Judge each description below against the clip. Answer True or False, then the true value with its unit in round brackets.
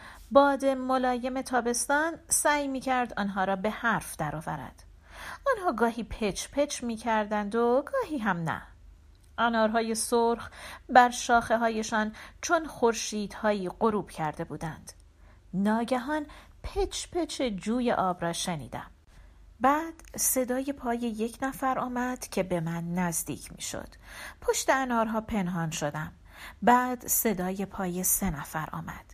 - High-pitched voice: True (230 Hz)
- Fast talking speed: False (125 wpm)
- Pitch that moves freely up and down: True (5.9 semitones)